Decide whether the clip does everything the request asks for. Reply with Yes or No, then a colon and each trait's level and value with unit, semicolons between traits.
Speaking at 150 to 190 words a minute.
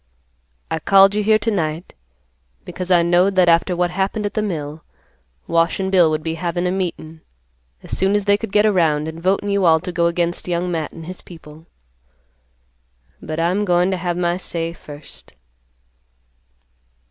Yes: average, 180 wpm